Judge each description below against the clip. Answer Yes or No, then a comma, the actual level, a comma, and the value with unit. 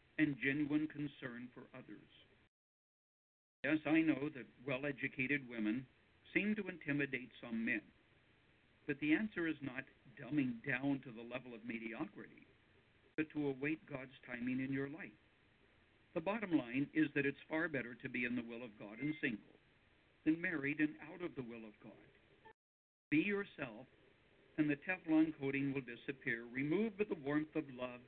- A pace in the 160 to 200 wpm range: Yes, average, 165 wpm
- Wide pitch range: No, average, 3.9 semitones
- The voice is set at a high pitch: No, medium, 140 Hz